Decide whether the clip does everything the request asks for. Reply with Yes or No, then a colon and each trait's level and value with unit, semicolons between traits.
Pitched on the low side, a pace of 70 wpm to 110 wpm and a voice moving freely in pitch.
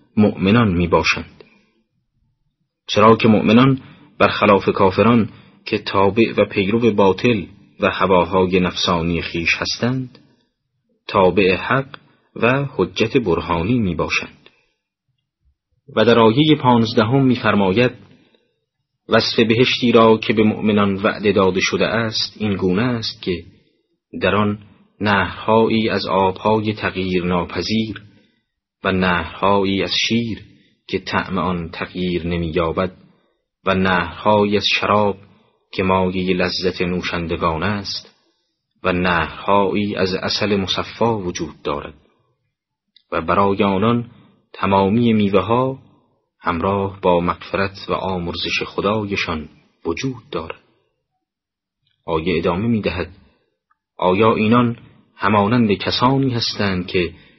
No: low, 100 Hz; slow, 105 wpm; average, 3.6 semitones